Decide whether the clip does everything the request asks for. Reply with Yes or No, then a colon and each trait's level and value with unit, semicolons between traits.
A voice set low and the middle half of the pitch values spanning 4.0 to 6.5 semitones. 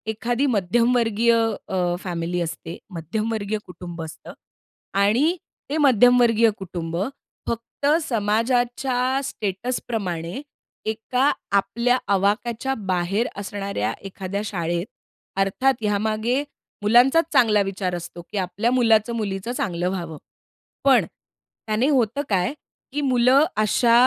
No: high, 215 Hz; average, 4.5 semitones